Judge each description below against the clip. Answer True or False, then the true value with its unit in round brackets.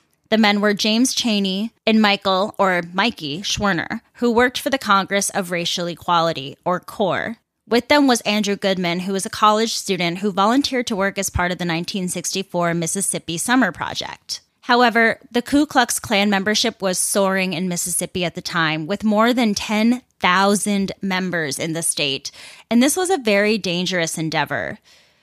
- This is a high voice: True (195 Hz)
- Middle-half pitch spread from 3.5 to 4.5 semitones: True (4.0 semitones)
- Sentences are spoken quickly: False (165 wpm)